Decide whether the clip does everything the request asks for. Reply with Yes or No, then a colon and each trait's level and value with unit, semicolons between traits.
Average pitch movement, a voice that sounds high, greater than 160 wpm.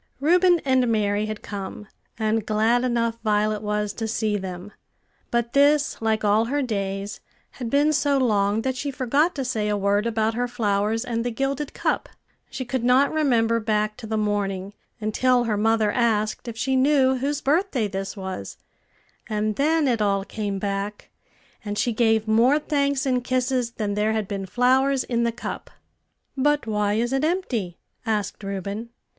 Yes: average, 3.8 semitones; high, 225 Hz; average, 175 wpm